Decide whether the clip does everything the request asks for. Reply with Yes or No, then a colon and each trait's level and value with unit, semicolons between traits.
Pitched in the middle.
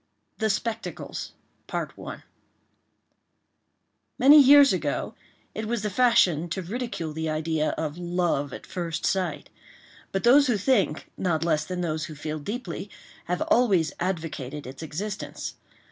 Yes: medium, 180 Hz